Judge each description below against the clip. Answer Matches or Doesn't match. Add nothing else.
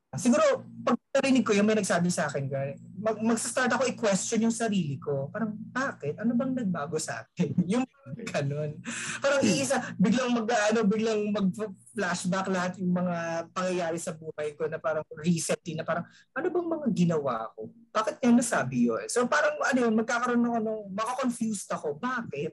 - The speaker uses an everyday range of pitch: Doesn't match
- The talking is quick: Matches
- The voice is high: Matches